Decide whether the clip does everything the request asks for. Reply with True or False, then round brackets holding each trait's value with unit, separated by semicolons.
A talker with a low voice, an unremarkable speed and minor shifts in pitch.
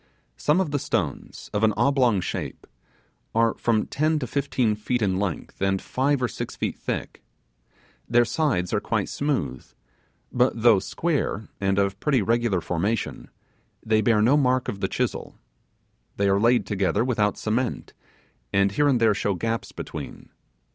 False (115 Hz; 160 wpm; 4.3 semitones)